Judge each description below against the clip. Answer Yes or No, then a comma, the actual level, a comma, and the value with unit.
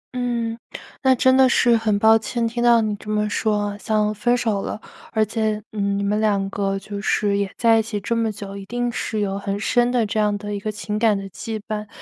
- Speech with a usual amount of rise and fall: No, narrow, 2.0 semitones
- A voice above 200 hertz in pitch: Yes, high, 215 Hz